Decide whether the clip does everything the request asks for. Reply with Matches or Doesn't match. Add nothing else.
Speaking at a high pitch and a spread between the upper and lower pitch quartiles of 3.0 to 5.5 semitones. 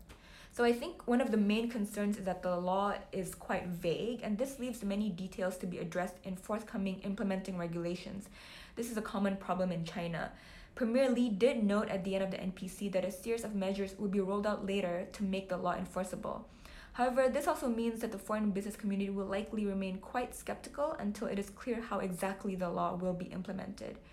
Doesn't match